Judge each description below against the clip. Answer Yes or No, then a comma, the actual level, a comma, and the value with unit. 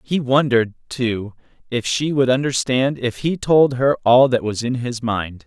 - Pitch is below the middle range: Yes, low, 125 Hz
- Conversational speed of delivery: Yes, average, 185 wpm